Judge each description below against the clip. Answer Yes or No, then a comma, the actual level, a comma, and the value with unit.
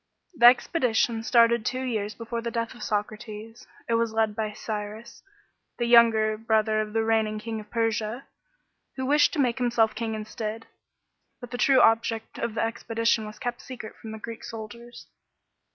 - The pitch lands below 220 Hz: No, high, 225 Hz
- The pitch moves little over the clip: Yes, narrow, 1.5 semitones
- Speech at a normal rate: Yes, average, 170 wpm